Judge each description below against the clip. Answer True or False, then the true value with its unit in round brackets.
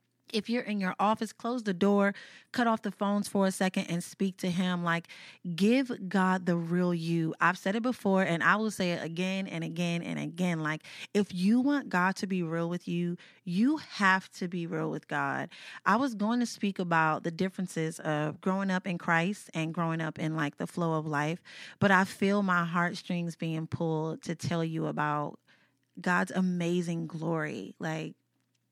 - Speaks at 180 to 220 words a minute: True (195 wpm)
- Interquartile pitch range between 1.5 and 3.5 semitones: True (3.1 semitones)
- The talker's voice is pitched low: False (180 Hz)